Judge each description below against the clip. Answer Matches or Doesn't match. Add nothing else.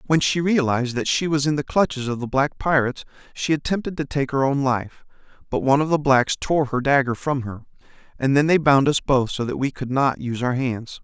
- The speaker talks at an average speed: Doesn't match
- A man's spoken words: Matches